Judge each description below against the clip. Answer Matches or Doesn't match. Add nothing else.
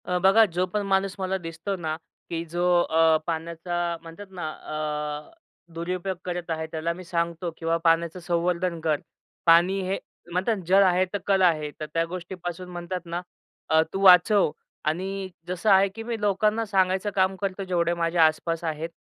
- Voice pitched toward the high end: Doesn't match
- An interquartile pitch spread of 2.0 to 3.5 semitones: Matches